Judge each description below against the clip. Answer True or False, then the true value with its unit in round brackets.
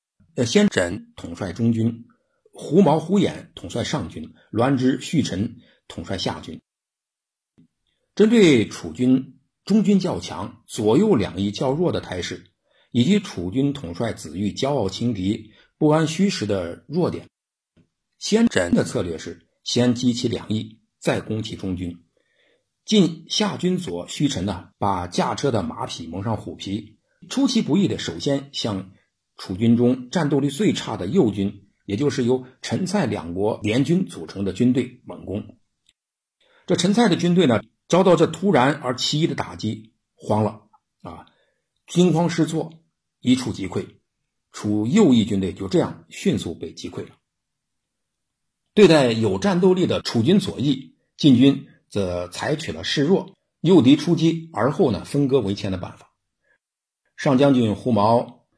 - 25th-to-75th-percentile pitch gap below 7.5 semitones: False (8.1 semitones)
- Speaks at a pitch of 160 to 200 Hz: False (125 Hz)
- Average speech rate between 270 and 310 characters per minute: False (215 characters per minute)